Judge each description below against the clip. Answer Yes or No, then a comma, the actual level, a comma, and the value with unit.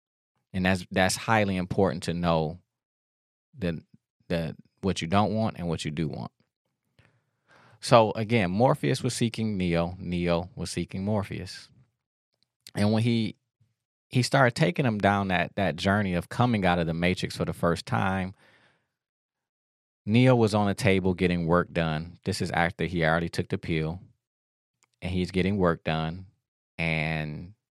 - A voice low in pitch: Yes, very low, 90 Hz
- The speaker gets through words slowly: No, average, 155 wpm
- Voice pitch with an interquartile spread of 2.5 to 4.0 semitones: No, average, 4.7 semitones